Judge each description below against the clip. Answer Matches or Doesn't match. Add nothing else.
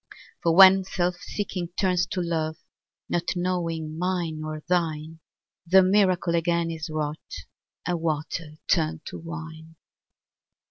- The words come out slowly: Matches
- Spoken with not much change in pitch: Matches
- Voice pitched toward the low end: Doesn't match